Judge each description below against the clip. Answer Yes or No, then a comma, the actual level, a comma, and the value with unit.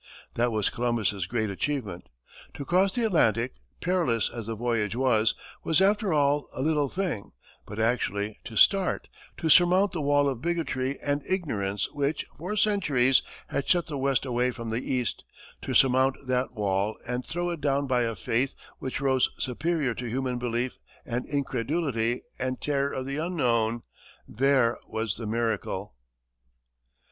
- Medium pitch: No, low, 130 Hz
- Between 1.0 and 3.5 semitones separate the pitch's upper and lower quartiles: No, average, 4.2 semitones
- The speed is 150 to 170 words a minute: Yes, average, 155 wpm